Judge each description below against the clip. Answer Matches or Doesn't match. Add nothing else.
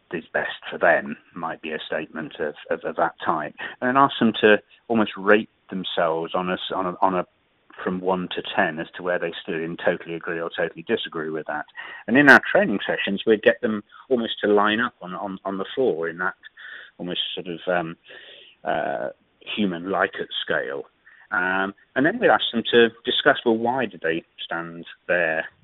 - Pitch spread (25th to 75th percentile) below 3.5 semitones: Doesn't match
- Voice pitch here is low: Matches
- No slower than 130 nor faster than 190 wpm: Doesn't match